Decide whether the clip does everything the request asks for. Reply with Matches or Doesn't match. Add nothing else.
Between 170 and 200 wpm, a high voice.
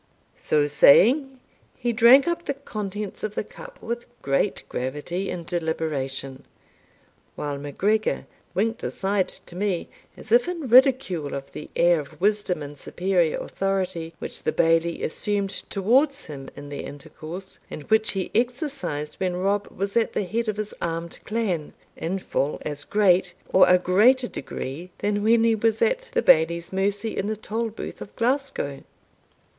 Doesn't match